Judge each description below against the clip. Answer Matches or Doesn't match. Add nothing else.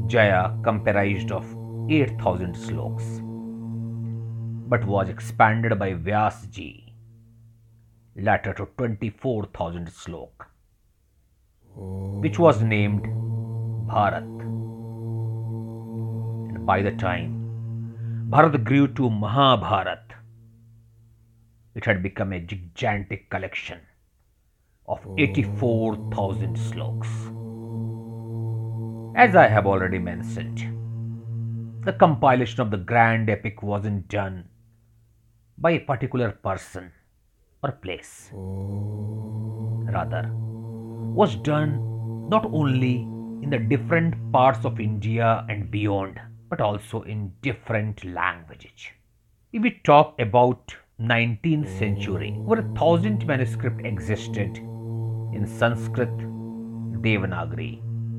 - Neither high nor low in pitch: Doesn't match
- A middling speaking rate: Doesn't match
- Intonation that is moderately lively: Doesn't match